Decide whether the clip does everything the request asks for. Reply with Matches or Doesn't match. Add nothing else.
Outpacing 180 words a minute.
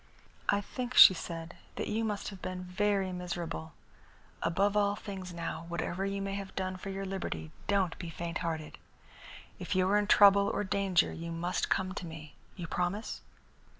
Doesn't match